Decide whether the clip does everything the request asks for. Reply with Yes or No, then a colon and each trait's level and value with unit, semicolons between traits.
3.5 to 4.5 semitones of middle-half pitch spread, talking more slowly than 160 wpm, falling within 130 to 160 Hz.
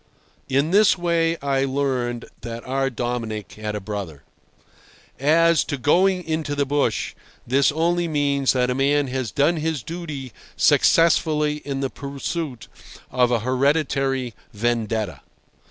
Yes: average, 4.2 semitones; slow, 135 wpm; medium, 140 Hz